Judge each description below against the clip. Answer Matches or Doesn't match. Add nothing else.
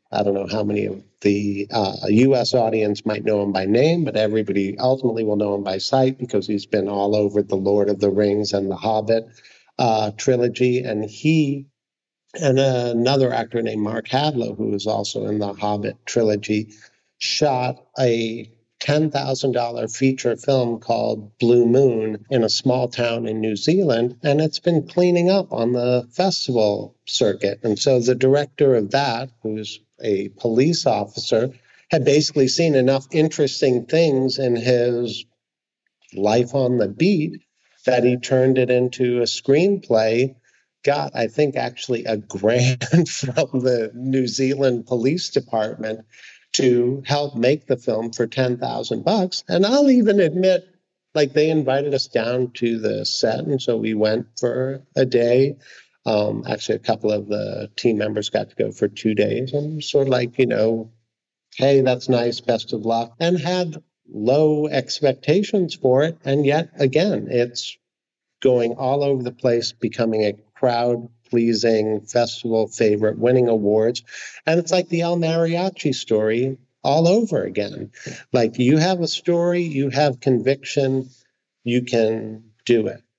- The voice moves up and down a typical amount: Matches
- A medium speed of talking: Matches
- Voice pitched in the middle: Doesn't match